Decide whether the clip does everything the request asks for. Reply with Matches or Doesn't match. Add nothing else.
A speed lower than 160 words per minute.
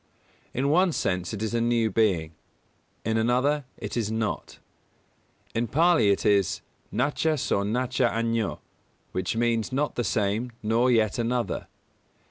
Matches